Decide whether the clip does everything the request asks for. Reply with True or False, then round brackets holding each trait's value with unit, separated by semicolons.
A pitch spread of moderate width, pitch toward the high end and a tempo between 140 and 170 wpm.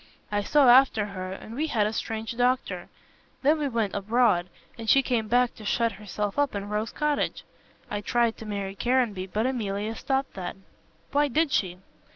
False (3.9 semitones; 225 Hz; 185 wpm)